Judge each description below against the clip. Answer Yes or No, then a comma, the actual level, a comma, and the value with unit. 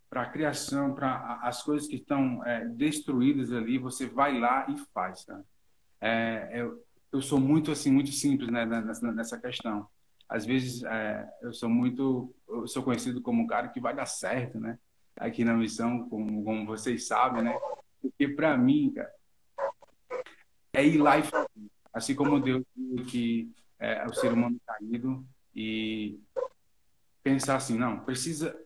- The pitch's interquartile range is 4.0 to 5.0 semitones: No, average, 3.4 semitones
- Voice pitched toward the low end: Yes, low, 125 Hz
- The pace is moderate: Yes, average, 155 wpm